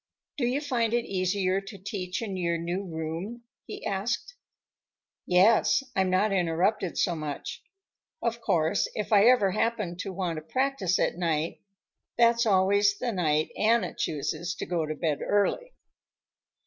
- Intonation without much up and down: No, average, 4.6 semitones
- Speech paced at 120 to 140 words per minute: No, average, 150 wpm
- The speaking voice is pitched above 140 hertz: Yes, high, 190 Hz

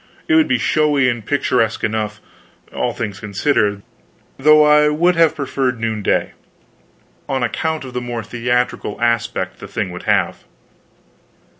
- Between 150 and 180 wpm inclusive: No, average, 140 wpm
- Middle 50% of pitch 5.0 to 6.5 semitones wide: Yes, wide, 5.6 semitones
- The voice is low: Yes, low, 120 Hz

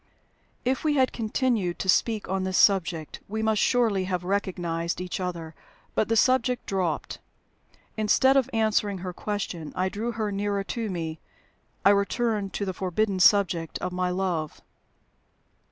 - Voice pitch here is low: No, high, 195 Hz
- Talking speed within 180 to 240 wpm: No, average, 155 wpm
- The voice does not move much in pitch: No, average, 3.3 semitones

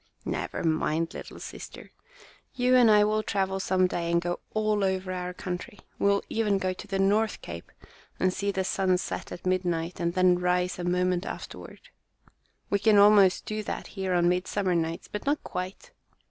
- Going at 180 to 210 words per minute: Yes, average, 185 wpm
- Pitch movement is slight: Yes, narrow, 2.2 semitones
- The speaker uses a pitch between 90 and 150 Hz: No, medium, 185 Hz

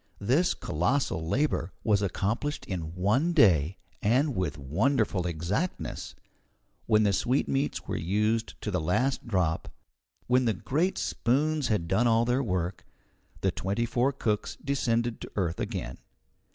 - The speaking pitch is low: Yes, low, 110 Hz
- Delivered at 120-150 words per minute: Yes, average, 140 wpm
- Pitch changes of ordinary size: No, wide, 6.1 semitones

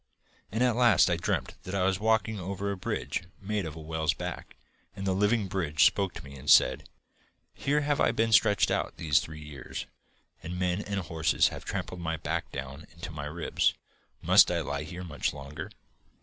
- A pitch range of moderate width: Yes, average, 4.5 semitones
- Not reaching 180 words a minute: No, average, 195 wpm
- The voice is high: No, very low, 90 Hz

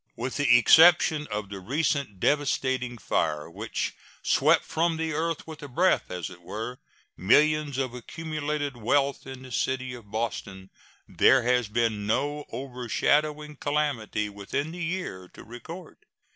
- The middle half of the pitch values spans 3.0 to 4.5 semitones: No, average, 5.1 semitones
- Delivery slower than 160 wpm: Yes, average, 145 wpm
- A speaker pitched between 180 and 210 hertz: No, low, 130 Hz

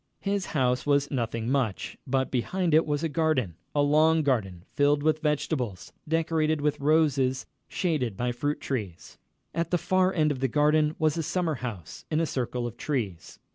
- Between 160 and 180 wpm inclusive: Yes, average, 175 wpm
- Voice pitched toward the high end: No, medium, 145 Hz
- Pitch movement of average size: Yes, average, 4.0 semitones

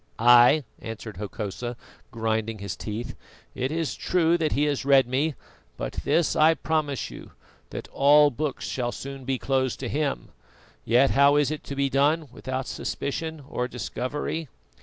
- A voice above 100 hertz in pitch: Yes, low, 135 Hz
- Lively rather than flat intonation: No, average, 3.6 semitones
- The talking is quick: No, average, 160 wpm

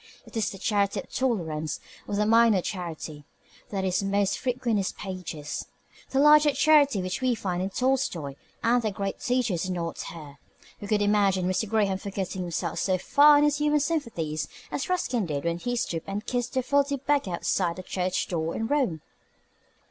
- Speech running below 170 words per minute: No, average, 190 wpm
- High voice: Yes, high, 200 Hz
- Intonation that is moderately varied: No, wide, 5.9 semitones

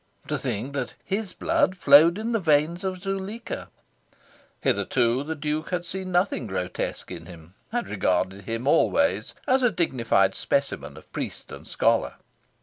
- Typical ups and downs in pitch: No, wide, 8.6 semitones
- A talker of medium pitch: Yes, medium, 160 Hz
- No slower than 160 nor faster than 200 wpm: No, average, 150 wpm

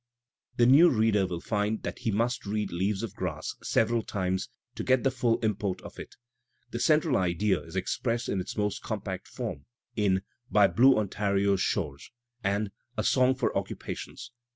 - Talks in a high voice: No, low, 105 Hz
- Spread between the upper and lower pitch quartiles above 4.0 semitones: No, average, 3.7 semitones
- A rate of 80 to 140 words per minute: No, average, 170 wpm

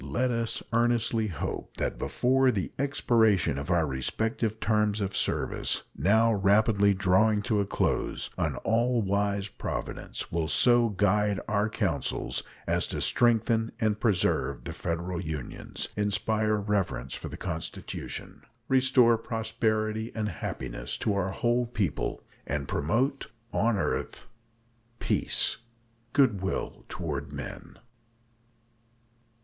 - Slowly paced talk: Yes, slow, 120 wpm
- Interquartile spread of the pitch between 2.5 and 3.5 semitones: Yes, average, 3.2 semitones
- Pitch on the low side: Yes, low, 105 Hz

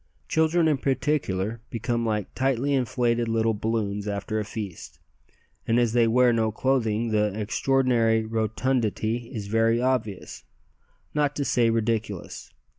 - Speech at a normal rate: No, slow, 130 wpm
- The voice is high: No, low, 115 Hz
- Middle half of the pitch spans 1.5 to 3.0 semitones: Yes, narrow, 2.6 semitones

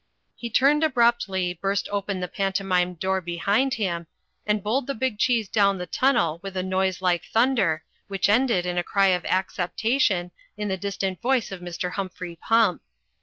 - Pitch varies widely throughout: No, average, 3.9 semitones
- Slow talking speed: No, average, 170 wpm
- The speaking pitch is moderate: No, high, 195 Hz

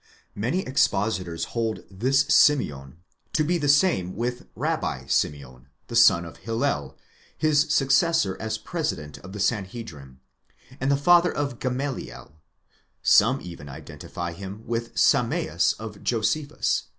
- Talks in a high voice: No, low, 115 Hz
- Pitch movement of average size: No, wide, 8.1 semitones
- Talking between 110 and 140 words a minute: Yes, slow, 135 wpm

